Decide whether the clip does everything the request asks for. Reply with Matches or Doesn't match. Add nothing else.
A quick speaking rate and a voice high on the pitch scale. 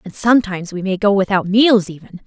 Matches